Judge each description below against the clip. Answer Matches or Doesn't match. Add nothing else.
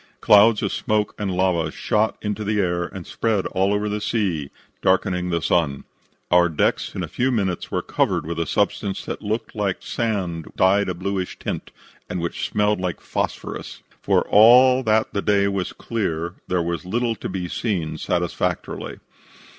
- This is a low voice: Matches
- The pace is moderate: Matches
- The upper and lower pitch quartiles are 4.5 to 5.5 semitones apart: Doesn't match